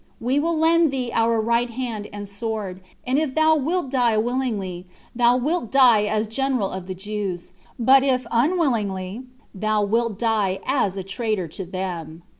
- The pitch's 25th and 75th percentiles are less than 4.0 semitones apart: No, average, 4.6 semitones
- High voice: Yes, high, 230 Hz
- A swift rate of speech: No, average, 170 wpm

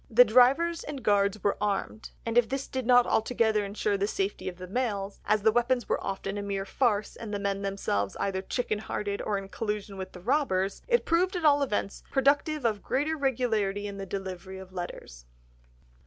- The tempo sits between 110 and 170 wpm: No, average, 190 wpm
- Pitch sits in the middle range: No, high, 210 Hz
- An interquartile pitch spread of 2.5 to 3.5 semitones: No, average, 4.2 semitones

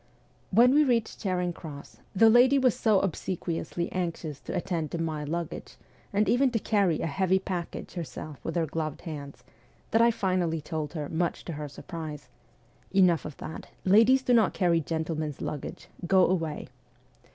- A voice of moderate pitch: Yes, medium, 175 Hz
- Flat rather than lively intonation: No, average, 4.1 semitones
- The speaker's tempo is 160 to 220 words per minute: Yes, average, 170 wpm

